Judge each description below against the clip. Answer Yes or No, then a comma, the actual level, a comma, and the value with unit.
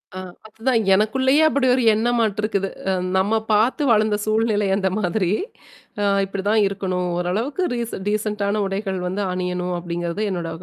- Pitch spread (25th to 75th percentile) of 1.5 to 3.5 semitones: Yes, average, 2.9 semitones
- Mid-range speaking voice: No, high, 210 Hz